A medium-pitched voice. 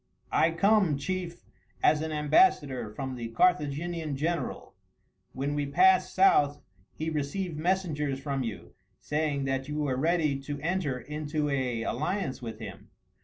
Yes: medium, 150 Hz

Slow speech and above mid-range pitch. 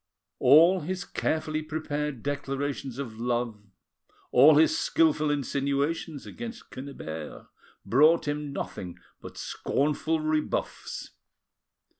No: slow, 95 wpm; medium, 145 Hz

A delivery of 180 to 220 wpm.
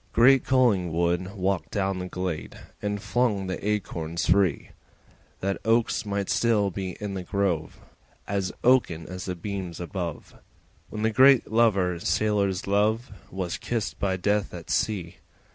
No: average, 145 wpm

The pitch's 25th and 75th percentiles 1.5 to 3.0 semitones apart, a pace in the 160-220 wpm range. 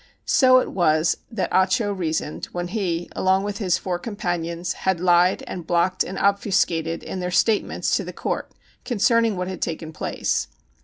Yes: average, 2.7 semitones; average, 170 wpm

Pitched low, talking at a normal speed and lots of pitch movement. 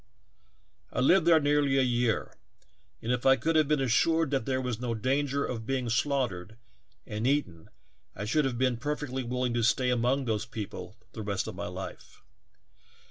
No: low, 125 Hz; average, 180 wpm; average, 3.5 semitones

